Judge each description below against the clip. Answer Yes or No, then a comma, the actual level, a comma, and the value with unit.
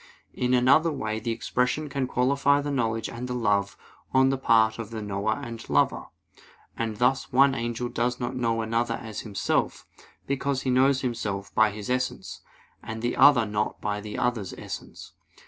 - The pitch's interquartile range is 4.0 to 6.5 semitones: No, average, 3.0 semitones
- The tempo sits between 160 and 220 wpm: Yes, average, 175 wpm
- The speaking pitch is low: Yes, low, 120 Hz